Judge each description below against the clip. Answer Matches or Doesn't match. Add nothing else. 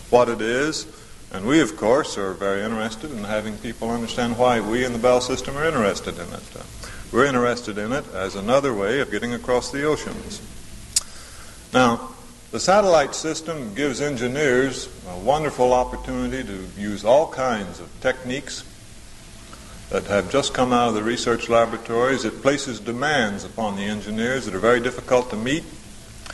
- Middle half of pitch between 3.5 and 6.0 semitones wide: Doesn't match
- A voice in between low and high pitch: Doesn't match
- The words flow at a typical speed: Matches